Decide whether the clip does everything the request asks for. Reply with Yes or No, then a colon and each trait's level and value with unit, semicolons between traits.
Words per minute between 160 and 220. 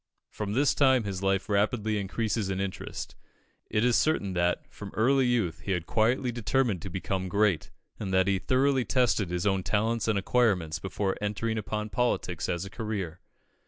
Yes: average, 175 wpm